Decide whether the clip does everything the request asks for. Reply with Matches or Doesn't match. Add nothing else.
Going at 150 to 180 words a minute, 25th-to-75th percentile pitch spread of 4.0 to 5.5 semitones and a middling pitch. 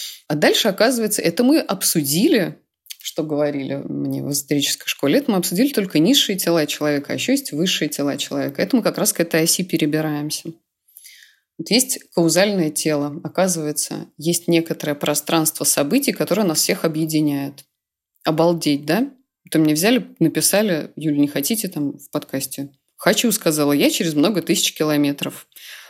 Matches